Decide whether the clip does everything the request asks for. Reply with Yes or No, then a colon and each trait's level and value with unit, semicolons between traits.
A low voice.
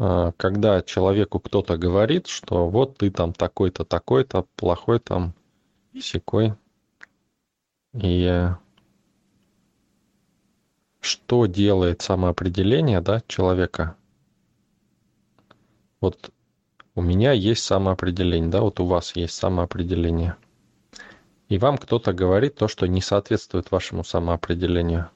Yes: very low, 95 Hz